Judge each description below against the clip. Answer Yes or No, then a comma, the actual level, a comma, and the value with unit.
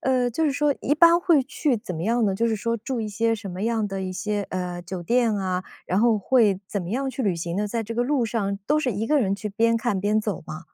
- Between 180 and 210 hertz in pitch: No, high, 220 Hz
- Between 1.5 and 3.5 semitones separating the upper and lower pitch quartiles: No, average, 4.0 semitones